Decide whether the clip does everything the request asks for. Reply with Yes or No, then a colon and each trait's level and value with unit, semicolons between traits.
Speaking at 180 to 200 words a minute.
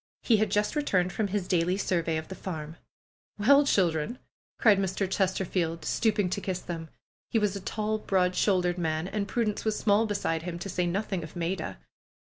Yes: average, 190 wpm